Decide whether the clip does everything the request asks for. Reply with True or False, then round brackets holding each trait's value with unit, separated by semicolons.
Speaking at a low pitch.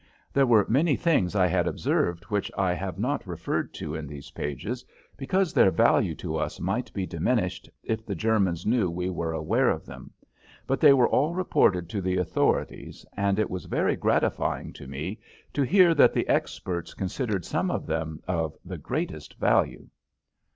True (95 Hz)